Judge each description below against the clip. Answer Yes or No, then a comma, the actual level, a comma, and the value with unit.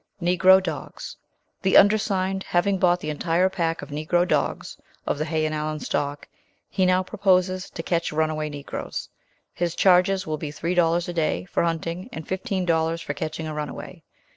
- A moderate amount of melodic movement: Yes, average, 3.1 semitones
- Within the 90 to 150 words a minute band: No, average, 175 wpm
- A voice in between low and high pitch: Yes, medium, 170 Hz